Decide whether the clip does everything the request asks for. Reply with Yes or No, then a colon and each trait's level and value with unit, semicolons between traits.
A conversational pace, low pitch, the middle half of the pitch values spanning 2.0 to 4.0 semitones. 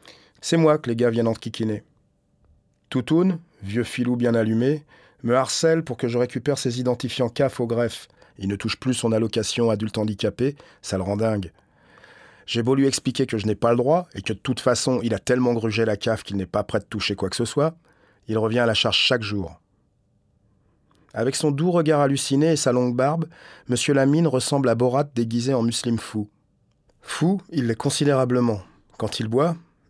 Yes: average, 200 wpm; low, 120 Hz; average, 3.7 semitones